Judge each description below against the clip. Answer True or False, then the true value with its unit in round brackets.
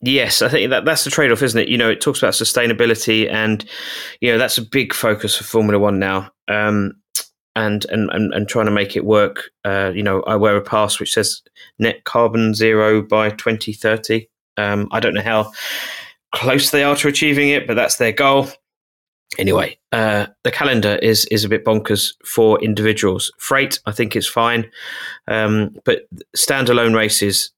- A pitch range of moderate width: False (1.6 semitones)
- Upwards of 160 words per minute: True (185 wpm)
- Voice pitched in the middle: False (110 Hz)